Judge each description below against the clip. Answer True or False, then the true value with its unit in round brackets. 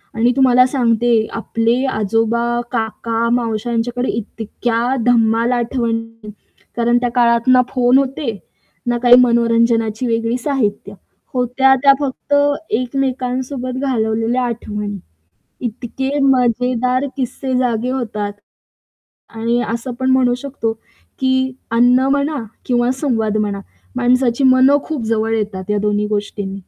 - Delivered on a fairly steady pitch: True (2.2 semitones)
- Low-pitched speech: False (240 Hz)